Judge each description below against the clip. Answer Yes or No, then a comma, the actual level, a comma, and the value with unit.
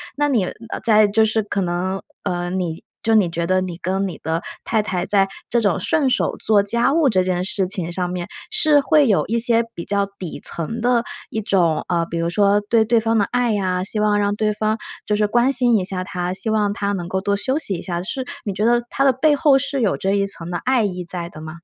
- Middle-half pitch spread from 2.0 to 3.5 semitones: No, average, 4.1 semitones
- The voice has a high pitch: Yes, high, 205 Hz